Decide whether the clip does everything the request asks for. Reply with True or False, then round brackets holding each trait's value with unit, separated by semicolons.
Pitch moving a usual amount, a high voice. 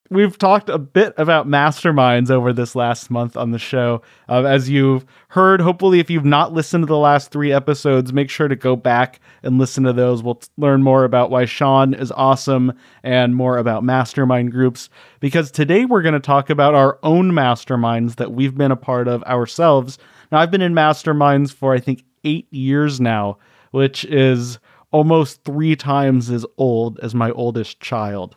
False (3.3 semitones; 135 Hz)